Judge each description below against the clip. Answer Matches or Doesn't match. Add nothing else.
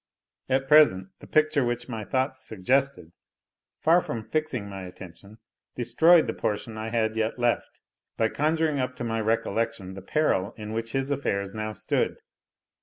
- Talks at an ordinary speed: Matches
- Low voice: Matches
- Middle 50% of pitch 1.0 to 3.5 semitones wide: Doesn't match